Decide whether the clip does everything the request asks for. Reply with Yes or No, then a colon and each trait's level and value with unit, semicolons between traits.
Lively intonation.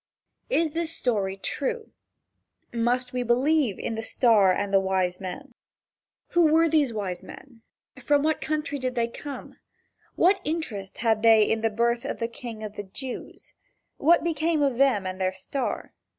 Yes: wide, 6.1 semitones